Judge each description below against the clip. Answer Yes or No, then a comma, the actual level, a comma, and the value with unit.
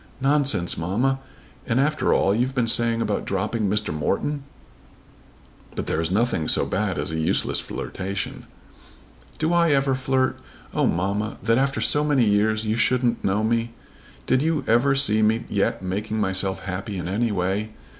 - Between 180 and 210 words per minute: No, average, 165 wpm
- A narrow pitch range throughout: No, average, 5.0 semitones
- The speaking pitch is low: Yes, low, 110 Hz